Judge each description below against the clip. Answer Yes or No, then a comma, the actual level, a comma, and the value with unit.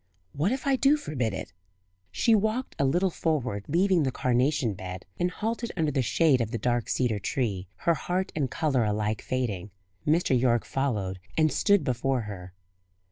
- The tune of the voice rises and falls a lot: Yes, wide, 7.4 semitones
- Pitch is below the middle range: Yes, low, 130 Hz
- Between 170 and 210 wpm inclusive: Yes, average, 175 wpm